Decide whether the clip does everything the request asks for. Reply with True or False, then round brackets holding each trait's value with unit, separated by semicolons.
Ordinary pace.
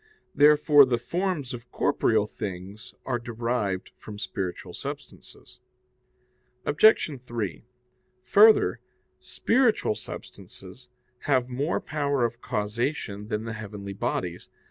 False (100 wpm)